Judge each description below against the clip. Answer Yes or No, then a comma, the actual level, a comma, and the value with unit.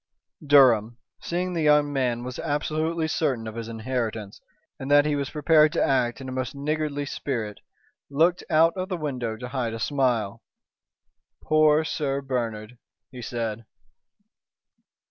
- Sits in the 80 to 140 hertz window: Yes, low, 135 Hz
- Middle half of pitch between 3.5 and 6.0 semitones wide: Yes, average, 4.4 semitones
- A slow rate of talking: No, average, 145 wpm